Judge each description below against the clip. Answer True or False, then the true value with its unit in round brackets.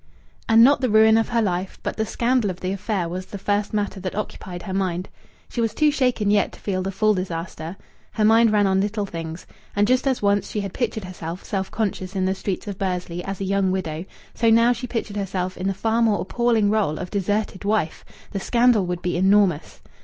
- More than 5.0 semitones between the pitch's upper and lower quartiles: False (3.0 semitones)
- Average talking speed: False (225 wpm)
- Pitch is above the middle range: True (200 Hz)